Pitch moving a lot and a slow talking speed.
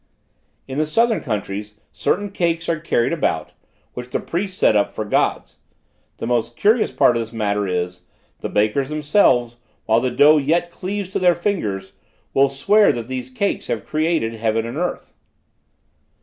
No: wide, 7.3 semitones; average, 165 wpm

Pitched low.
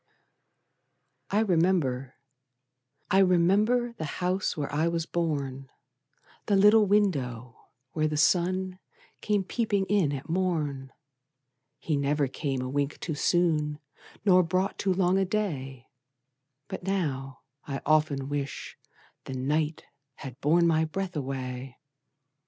No: medium, 160 Hz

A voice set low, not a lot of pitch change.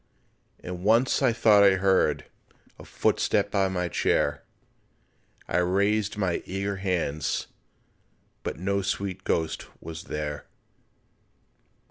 Yes: very low, 95 Hz; narrow, 2.1 semitones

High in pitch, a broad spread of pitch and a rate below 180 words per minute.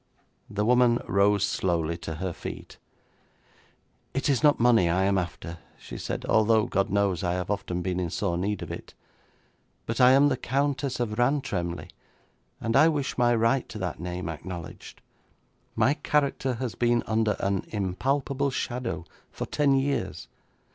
No: low, 110 Hz; wide, 6.1 semitones; average, 160 wpm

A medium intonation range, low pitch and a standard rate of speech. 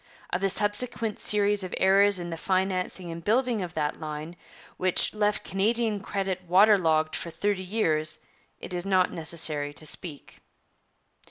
No: average, 3.8 semitones; medium, 185 Hz; average, 155 wpm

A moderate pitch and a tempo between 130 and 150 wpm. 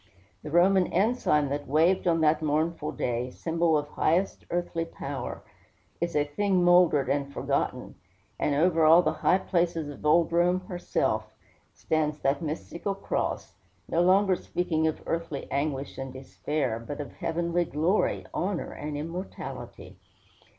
Yes: medium, 165 Hz; average, 145 wpm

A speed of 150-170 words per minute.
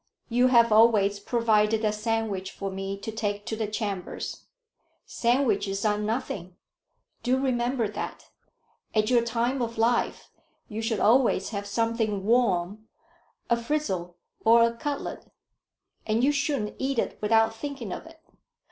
No: average, 140 wpm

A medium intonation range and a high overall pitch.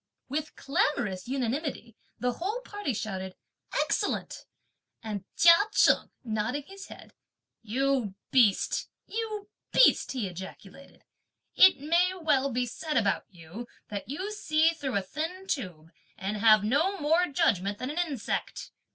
No: wide, 7.6 semitones; very high, 265 Hz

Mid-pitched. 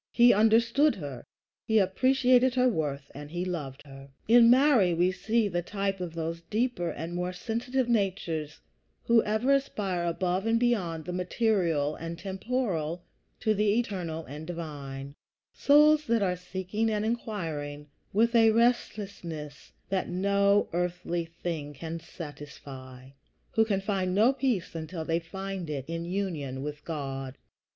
Yes: medium, 180 Hz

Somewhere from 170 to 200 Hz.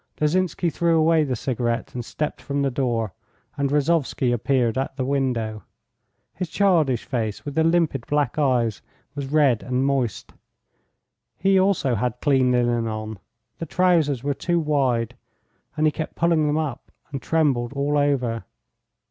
No: medium, 140 Hz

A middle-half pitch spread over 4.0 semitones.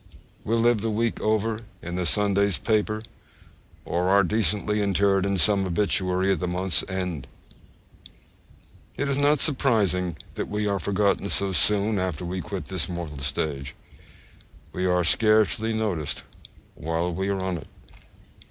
No: average, 3.1 semitones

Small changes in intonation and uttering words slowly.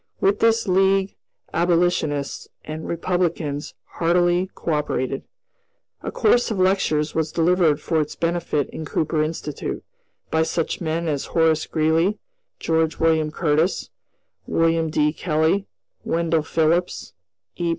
Yes: narrow, 2.3 semitones; slow, 120 wpm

